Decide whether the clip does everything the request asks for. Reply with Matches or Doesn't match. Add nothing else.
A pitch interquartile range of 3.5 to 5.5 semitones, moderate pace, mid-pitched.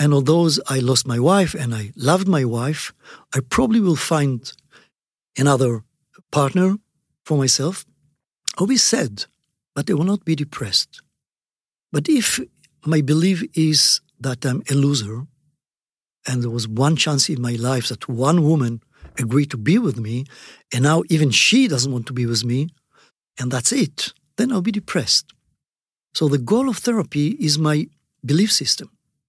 Matches